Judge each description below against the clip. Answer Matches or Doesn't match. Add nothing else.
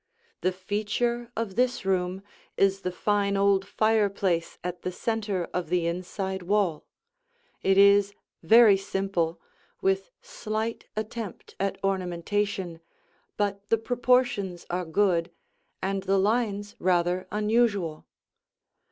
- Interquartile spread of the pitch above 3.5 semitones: Doesn't match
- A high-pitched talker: Matches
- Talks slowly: Matches